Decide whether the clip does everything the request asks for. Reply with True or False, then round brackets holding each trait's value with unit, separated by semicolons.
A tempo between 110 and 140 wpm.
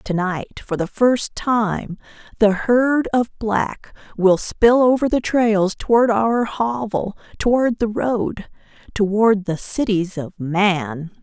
True (135 wpm)